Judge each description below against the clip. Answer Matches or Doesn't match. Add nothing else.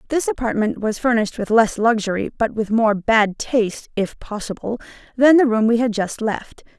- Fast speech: Doesn't match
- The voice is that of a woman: Matches